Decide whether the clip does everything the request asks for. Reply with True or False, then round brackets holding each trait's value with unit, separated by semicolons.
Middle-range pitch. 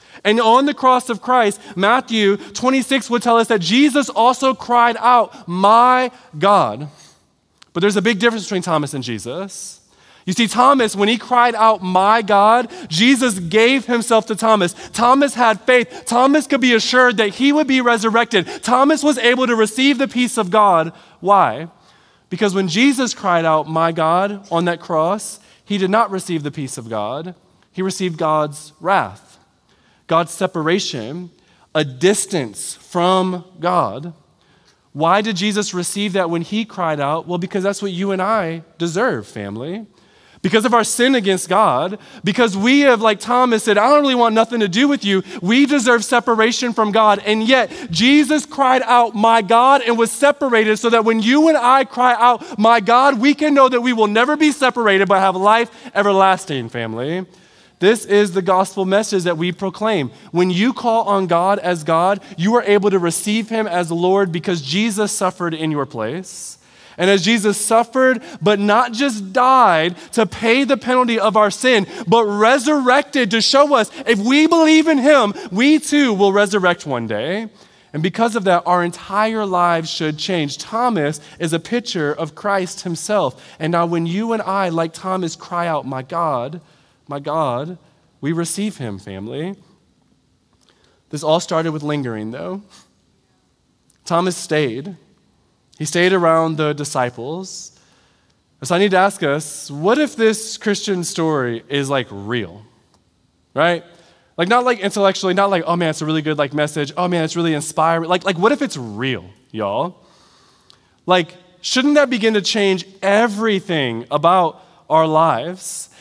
False (200 Hz)